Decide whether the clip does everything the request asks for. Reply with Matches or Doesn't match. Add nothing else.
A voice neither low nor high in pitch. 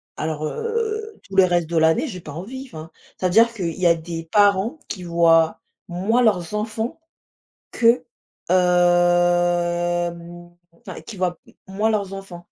Matches